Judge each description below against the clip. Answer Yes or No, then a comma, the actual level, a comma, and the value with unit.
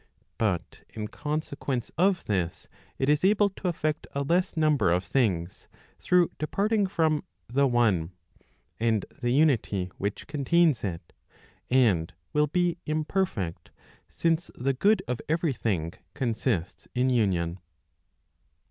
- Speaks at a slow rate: Yes, slow, 125 wpm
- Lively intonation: Yes, wide, 7.8 semitones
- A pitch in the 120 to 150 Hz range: Yes, low, 135 Hz